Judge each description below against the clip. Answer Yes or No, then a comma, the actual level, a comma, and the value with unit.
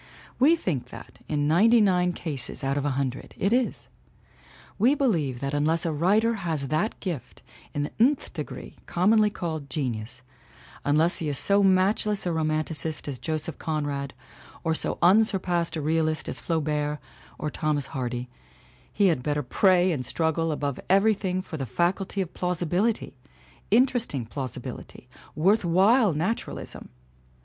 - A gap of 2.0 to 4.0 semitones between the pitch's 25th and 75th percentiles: No, average, 5.0 semitones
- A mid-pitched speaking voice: Yes, medium, 165 Hz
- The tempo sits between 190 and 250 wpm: No, average, 155 wpm